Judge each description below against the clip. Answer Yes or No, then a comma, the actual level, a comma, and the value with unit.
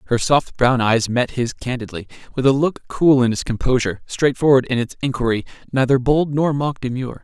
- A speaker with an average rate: Yes, average, 190 wpm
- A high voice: No, low, 130 Hz